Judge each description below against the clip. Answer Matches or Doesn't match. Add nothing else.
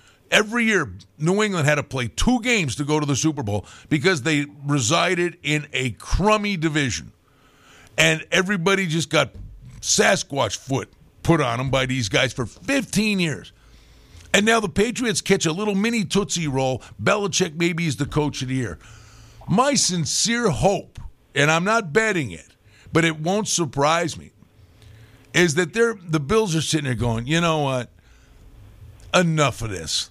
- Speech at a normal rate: Matches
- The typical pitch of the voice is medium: Matches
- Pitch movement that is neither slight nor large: Doesn't match